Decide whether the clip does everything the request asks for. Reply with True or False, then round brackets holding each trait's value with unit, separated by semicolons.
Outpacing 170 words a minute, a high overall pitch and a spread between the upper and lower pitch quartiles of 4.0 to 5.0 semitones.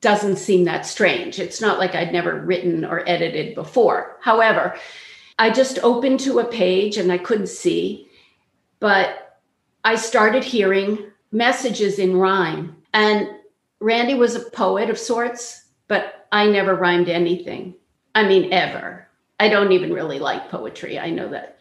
False (155 wpm; 205 Hz; 4.3 semitones)